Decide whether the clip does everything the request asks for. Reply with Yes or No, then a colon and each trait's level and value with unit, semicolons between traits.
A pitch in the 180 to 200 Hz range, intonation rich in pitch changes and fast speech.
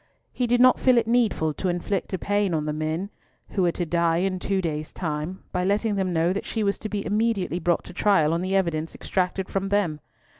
No: medium, 185 Hz; average, 3.3 semitones; fast, 230 wpm